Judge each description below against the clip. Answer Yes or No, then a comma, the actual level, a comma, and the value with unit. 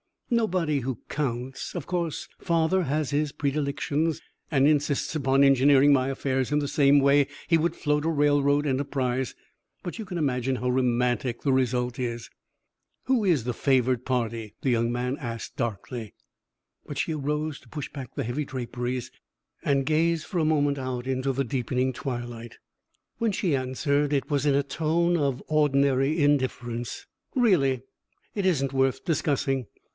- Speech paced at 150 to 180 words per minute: Yes, average, 160 wpm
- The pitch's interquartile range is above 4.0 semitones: No, average, 3.0 semitones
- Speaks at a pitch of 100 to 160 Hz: Yes, medium, 140 Hz